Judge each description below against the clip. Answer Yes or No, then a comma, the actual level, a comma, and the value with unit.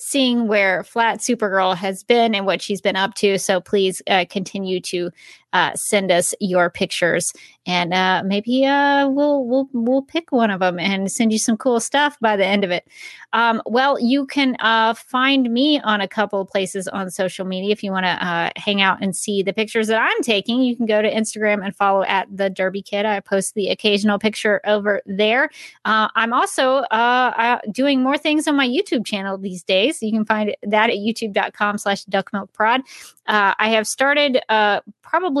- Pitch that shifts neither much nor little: Yes, average, 3.7 semitones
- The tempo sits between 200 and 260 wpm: Yes, fast, 205 wpm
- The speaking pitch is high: Yes, high, 210 Hz